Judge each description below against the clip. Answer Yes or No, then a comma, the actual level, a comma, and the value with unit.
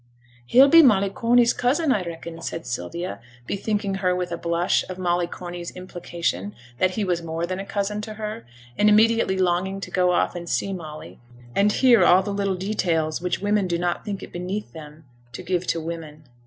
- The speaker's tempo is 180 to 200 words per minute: Yes, average, 195 wpm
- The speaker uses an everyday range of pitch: Yes, average, 3.1 semitones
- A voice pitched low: No, medium, 185 Hz